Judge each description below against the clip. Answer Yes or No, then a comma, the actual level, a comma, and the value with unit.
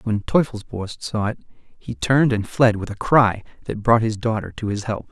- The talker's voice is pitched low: Yes, low, 110 Hz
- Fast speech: Yes, fast, 210 wpm